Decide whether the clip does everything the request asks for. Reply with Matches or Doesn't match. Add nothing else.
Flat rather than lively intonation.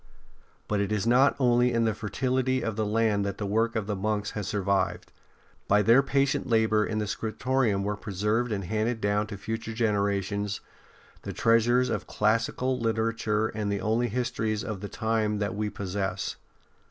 Matches